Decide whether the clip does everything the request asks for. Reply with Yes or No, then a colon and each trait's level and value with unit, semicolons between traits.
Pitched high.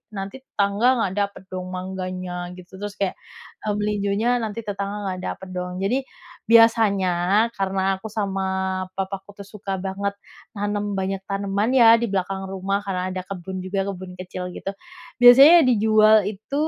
Yes: high, 195 Hz